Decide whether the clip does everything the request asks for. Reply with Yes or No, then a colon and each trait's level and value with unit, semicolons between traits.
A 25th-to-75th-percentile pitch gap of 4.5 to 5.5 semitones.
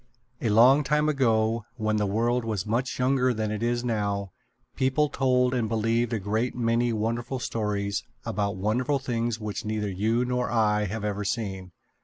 No: average, 2.9 semitones